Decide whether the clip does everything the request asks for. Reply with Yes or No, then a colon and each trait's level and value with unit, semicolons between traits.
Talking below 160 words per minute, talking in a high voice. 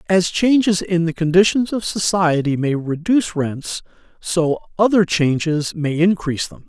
No: average, 145 wpm; medium, 175 Hz